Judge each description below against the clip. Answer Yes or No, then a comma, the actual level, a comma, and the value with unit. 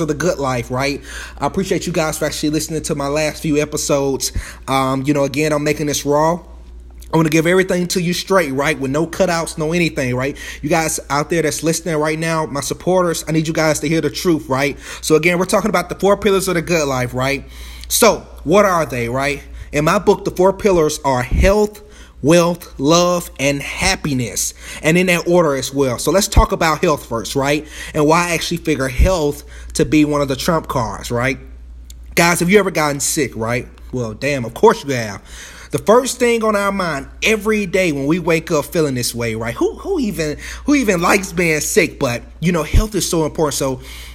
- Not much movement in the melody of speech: No, average, 4.2 semitones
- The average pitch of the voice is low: No, medium, 155 Hz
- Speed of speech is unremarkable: No, fast, 220 wpm